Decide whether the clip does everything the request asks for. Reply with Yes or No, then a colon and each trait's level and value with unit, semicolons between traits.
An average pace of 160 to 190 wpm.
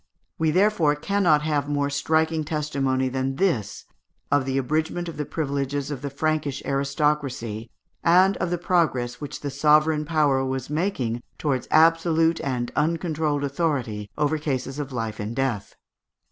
No: average, 145 wpm